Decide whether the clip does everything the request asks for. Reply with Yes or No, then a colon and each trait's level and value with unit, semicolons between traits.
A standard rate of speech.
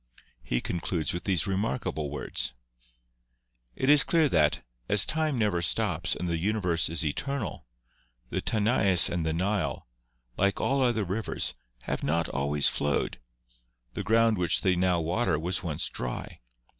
Yes: average, 150 wpm